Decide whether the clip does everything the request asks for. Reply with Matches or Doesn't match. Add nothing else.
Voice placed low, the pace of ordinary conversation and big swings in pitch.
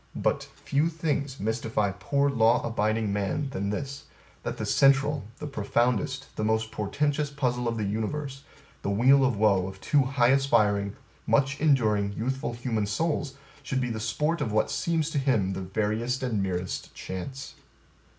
Doesn't match